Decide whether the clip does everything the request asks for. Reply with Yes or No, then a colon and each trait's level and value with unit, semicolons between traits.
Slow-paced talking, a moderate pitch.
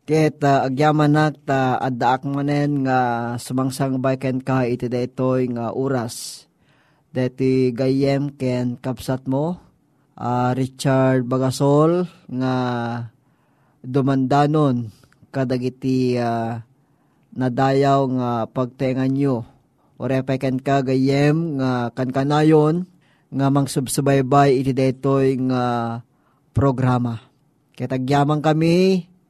No: slow, 100 wpm; low, 130 Hz